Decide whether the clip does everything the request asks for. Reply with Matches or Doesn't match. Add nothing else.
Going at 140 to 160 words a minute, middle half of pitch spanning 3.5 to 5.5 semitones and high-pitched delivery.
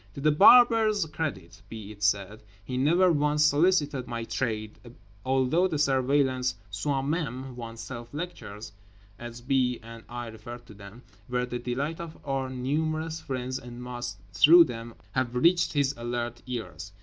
Doesn't match